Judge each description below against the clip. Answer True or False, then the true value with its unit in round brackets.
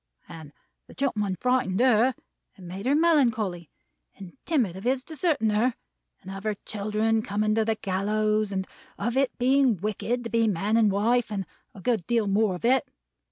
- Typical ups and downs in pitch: True (3.7 semitones)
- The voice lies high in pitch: True (215 Hz)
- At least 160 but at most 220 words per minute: True (180 wpm)